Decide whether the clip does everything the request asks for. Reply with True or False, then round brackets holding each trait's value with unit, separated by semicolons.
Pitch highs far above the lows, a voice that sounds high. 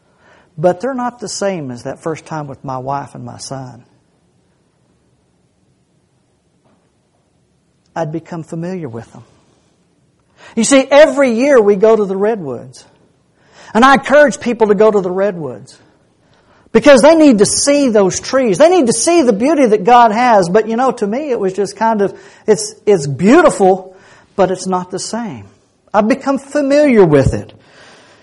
True (7.9 semitones; 200 Hz)